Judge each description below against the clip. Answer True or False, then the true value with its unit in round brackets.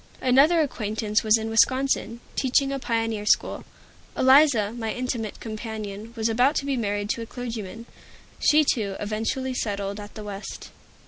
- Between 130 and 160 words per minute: True (150 wpm)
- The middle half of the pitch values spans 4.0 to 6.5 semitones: False (3.4 semitones)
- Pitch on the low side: False (225 Hz)